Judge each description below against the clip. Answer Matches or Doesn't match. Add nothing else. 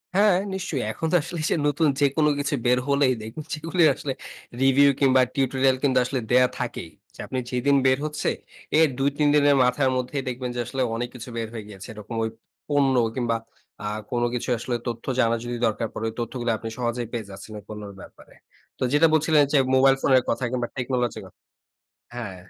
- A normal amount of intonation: Matches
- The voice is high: Doesn't match